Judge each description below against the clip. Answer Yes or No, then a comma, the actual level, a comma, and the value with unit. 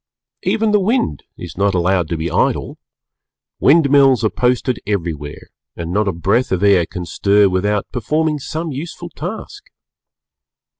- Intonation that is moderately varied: No, wide, 8.6 semitones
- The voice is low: Yes, low, 105 Hz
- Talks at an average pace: Yes, average, 150 wpm